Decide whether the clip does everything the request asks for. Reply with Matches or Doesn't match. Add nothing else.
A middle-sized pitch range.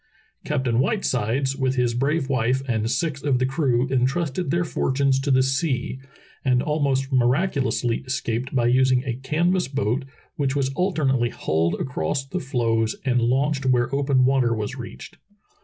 Doesn't match